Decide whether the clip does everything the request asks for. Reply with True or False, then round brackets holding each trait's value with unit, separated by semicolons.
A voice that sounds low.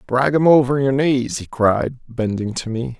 True (125 Hz)